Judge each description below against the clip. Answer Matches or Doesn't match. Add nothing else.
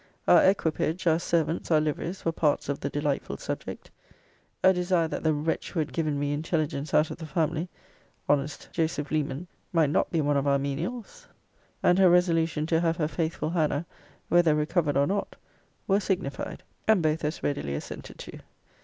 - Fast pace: Doesn't match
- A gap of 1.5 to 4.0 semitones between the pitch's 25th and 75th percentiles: Matches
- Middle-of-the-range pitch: Matches